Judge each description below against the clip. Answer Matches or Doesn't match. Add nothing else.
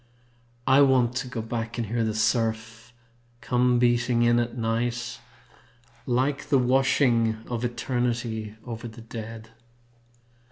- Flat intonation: Matches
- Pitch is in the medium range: Doesn't match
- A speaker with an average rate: Doesn't match